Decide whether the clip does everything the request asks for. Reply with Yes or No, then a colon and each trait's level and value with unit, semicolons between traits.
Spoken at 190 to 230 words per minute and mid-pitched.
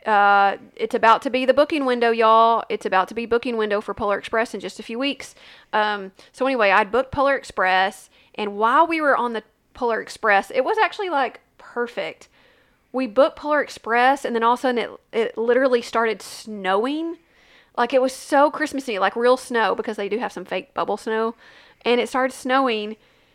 No: average, 200 wpm; high, 235 Hz